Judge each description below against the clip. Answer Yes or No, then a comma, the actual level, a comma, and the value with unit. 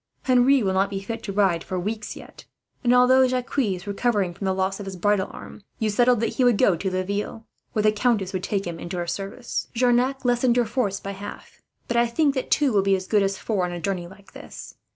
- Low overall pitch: No, high, 205 Hz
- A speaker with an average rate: No, fast, 250 wpm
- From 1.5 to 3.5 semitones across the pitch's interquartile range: No, average, 4.1 semitones